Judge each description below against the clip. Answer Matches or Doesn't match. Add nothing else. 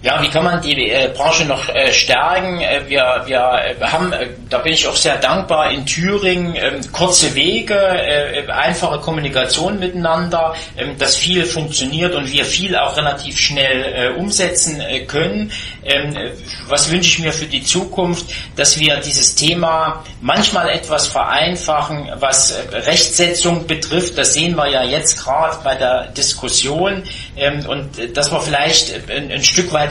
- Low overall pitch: Doesn't match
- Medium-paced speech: Matches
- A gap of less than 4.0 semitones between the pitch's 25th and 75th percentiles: Matches